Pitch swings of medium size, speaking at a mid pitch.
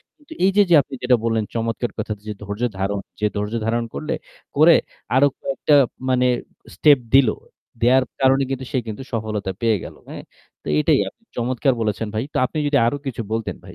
No: average, 3.7 semitones; low, 120 Hz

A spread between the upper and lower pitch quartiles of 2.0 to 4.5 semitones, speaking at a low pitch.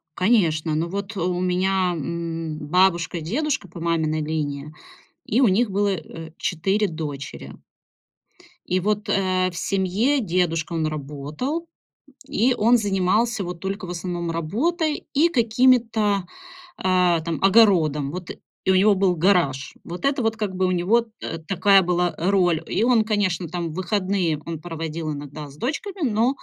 No: average, 4.2 semitones; medium, 185 Hz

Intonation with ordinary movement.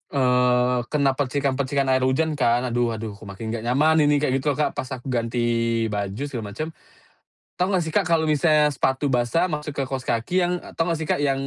Yes: average, 3.5 semitones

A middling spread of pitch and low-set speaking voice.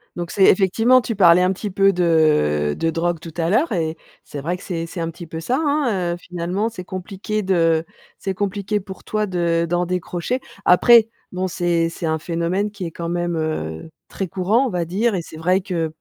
No: average, 3.0 semitones; medium, 180 Hz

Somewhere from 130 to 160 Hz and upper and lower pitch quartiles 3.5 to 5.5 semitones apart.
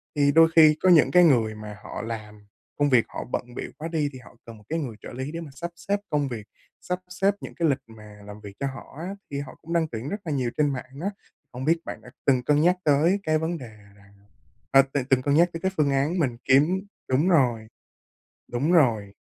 Yes: medium, 140 Hz; average, 5.2 semitones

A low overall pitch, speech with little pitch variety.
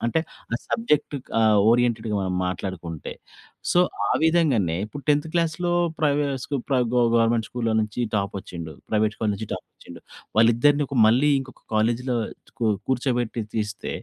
No: low, 115 Hz; average, 5.1 semitones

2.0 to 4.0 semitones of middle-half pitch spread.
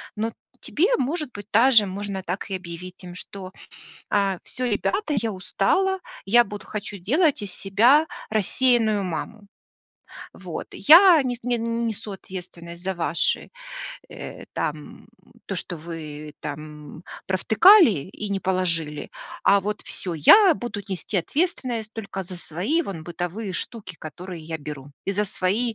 No: average, 4.9 semitones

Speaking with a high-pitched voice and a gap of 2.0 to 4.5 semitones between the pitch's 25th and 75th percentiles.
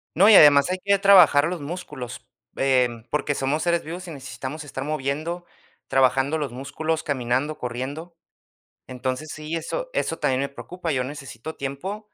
No: medium, 145 Hz; average, 4.0 semitones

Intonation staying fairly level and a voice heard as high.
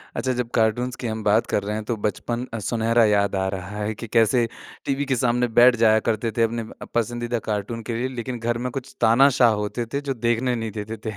No: narrow, 2.0 semitones; low, 115 Hz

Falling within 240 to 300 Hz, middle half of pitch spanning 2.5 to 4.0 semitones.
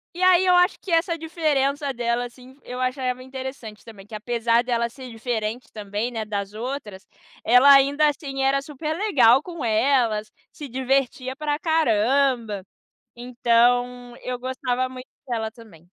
Yes: very high, 250 Hz; average, 3.1 semitones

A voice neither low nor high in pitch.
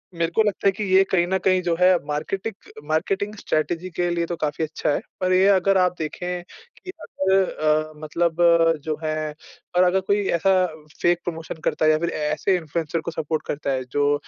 Yes: medium, 175 Hz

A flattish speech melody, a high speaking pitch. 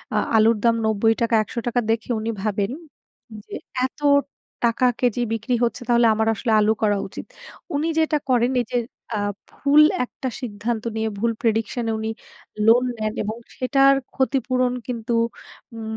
Yes: narrow, 2.2 semitones; high, 230 Hz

